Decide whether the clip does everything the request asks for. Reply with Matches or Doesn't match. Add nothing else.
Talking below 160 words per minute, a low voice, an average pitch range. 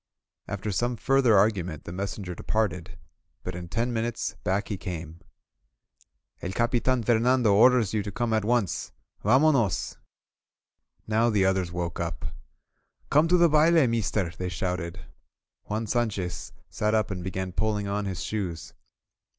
Matches